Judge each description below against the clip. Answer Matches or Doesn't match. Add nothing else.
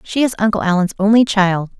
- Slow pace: Doesn't match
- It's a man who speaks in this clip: Doesn't match